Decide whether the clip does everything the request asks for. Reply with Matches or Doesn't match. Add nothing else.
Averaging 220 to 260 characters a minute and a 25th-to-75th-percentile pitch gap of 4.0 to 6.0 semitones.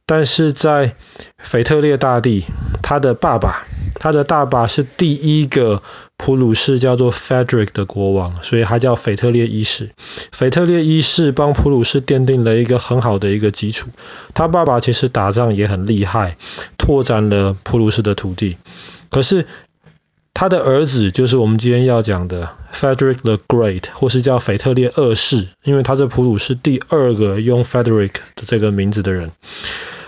Doesn't match